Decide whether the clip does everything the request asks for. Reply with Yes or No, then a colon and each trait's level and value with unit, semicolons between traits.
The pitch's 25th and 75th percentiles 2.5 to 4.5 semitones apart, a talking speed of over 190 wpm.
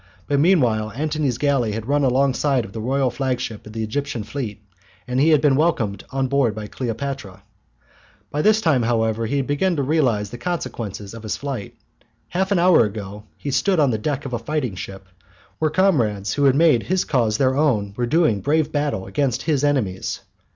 No: average, 5.0 semitones; average, 200 wpm